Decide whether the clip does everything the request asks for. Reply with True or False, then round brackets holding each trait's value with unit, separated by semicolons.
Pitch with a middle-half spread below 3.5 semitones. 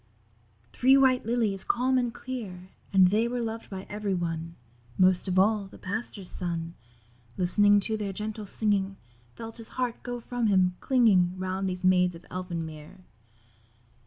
False (3.8 semitones)